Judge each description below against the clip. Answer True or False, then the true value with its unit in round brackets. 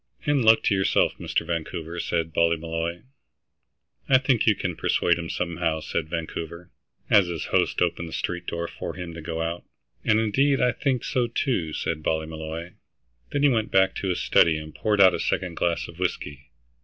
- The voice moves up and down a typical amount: True (4.2 semitones)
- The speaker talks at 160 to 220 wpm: True (185 wpm)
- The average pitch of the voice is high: False (85 Hz)